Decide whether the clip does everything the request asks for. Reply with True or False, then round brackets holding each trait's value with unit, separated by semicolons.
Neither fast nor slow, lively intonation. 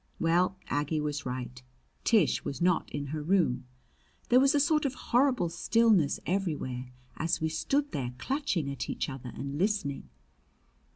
True (155 wpm; 7.6 semitones)